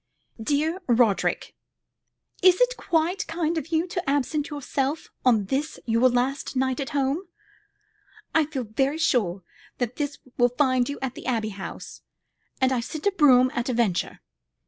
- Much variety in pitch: No, average, 4.3 semitones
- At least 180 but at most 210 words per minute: No, average, 160 wpm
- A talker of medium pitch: No, very high, 270 Hz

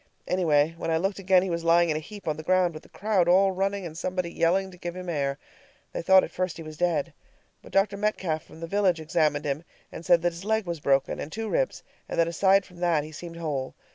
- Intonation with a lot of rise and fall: No, average, 3.1 semitones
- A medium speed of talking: No, fast, 250 wpm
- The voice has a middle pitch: Yes, medium, 175 Hz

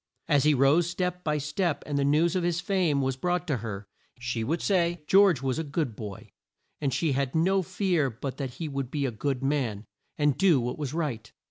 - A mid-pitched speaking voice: Yes, medium, 145 Hz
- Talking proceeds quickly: Yes, fast, 220 wpm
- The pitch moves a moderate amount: Yes, average, 4.6 semitones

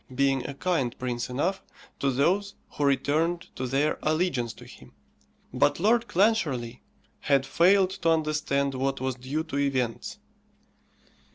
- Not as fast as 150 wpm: Yes, average, 140 wpm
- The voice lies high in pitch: No, medium, 140 Hz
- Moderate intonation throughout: Yes, average, 4.5 semitones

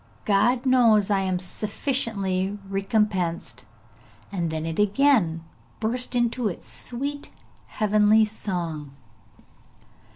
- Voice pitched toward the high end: Yes, high, 210 Hz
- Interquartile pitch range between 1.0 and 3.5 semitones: No, average, 4.3 semitones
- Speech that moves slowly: Yes, slow, 95 wpm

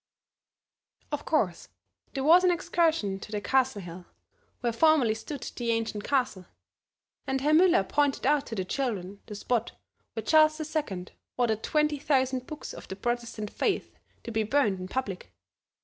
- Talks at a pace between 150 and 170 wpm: Yes, average, 160 wpm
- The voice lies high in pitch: Yes, high, 245 Hz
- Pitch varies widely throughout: Yes, wide, 6.0 semitones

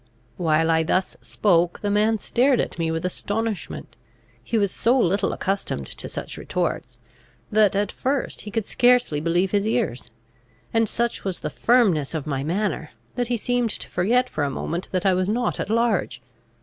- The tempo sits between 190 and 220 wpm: No, average, 180 wpm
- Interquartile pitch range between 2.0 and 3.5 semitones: No, average, 5.3 semitones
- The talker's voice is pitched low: No, high, 200 Hz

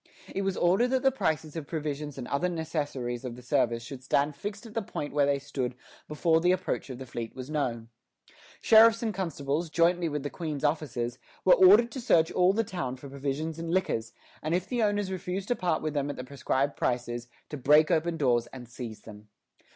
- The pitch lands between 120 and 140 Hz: No, medium, 150 Hz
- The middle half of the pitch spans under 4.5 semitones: No, wide, 5.5 semitones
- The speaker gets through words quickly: Yes, fast, 215 wpm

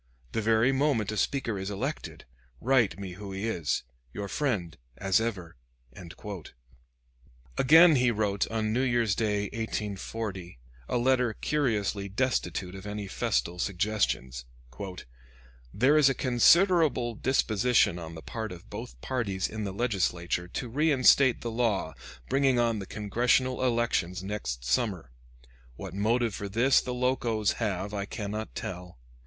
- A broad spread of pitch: No, average, 4.3 semitones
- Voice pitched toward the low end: Yes, low, 110 Hz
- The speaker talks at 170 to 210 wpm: No, slow, 135 wpm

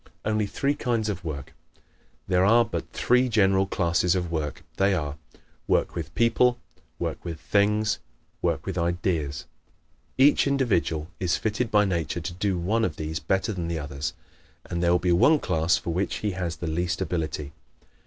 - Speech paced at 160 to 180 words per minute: Yes, average, 175 wpm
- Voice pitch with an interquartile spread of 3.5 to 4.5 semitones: Yes, average, 4.2 semitones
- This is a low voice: Yes, very low, 90 Hz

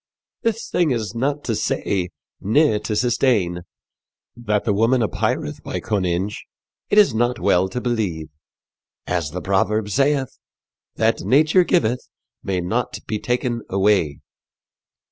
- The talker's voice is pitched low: Yes, low, 110 Hz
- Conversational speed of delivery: No, slow, 130 wpm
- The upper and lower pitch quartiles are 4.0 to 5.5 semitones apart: Yes, average, 4.7 semitones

